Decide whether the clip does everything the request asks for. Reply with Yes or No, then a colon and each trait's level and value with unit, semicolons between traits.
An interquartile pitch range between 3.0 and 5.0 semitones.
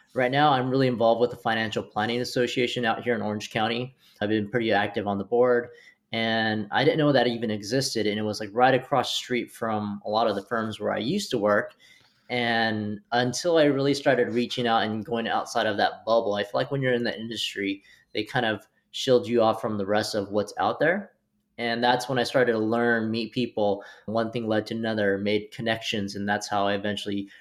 No: narrow, 2.5 semitones